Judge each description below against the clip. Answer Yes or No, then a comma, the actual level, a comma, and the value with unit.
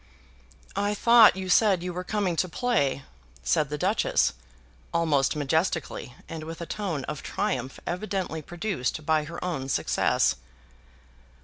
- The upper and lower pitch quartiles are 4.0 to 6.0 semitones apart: Yes, average, 4.4 semitones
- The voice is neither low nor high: Yes, medium, 170 Hz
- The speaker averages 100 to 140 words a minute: Yes, slow, 135 wpm